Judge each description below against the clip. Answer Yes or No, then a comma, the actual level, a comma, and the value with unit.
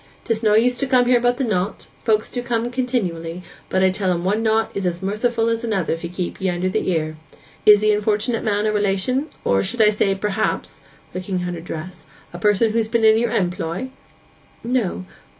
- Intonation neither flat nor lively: Yes, average, 3.8 semitones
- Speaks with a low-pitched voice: No, high, 210 Hz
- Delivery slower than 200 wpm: No, fast, 205 wpm